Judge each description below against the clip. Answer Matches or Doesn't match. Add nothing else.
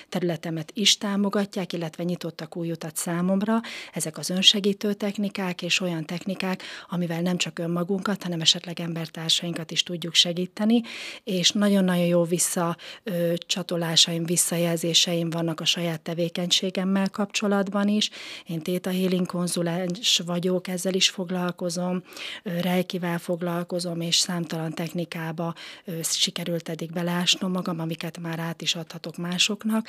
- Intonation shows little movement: Matches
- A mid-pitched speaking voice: Matches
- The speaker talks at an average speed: Matches